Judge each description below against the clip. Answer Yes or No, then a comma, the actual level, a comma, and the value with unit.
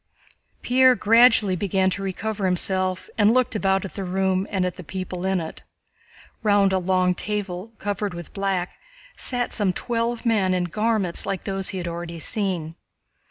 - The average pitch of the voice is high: Yes, high, 195 Hz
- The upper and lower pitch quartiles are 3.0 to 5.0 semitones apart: No, narrow, 2.6 semitones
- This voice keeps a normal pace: Yes, average, 165 wpm